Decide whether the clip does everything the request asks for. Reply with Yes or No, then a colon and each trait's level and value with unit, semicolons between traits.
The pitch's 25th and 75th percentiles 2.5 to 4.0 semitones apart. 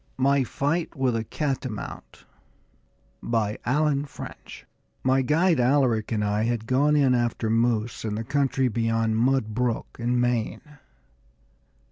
Yes: average, 3.5 semitones